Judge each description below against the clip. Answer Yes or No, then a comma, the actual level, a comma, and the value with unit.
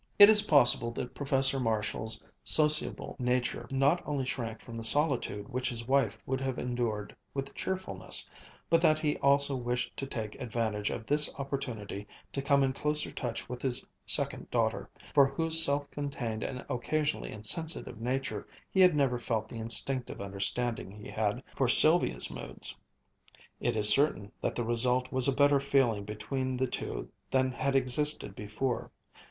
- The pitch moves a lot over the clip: No, average, 3.7 semitones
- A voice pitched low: Yes, low, 130 Hz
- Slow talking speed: No, average, 160 wpm